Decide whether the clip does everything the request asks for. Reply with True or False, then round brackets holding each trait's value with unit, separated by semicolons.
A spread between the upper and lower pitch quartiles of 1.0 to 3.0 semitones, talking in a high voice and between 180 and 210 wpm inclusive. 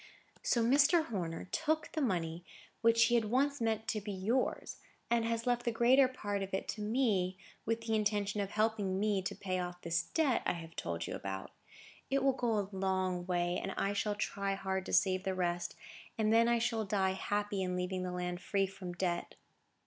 False (3.7 semitones; 205 Hz; 200 wpm)